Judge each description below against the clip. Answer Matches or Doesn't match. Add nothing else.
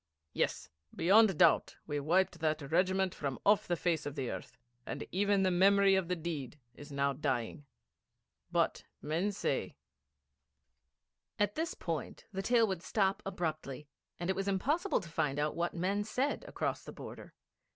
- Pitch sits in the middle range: Matches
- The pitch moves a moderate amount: Matches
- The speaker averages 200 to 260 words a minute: Doesn't match